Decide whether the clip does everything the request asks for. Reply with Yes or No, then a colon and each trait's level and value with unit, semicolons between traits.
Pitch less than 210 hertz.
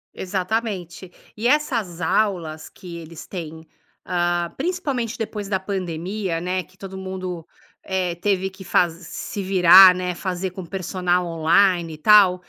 Yes: medium, 185 Hz